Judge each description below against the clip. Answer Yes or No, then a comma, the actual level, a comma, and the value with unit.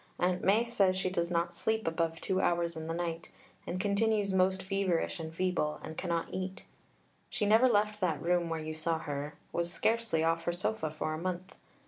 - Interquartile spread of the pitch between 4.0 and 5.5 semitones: No, average, 2.9 semitones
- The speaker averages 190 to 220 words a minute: Yes, average, 195 wpm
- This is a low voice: No, medium, 175 Hz